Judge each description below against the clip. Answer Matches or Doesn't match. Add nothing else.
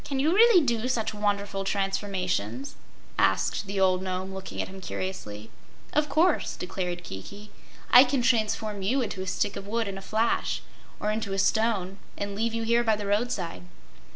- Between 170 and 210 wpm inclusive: Matches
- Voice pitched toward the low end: Doesn't match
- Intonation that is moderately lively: Matches